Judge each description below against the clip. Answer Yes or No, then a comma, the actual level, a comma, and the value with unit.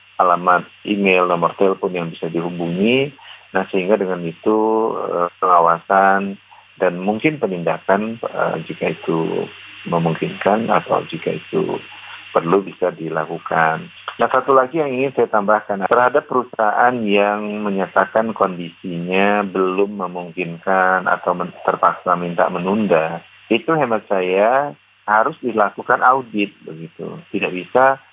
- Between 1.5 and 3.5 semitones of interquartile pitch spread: No, average, 4.0 semitones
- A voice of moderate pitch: No, low, 100 Hz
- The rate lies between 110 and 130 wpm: Yes, average, 115 wpm